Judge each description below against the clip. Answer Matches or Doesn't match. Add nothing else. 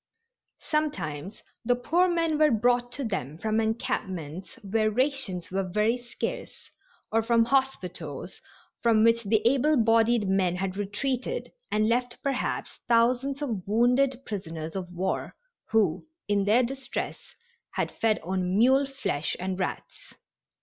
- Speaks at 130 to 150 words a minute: Matches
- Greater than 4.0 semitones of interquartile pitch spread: Matches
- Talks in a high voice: Matches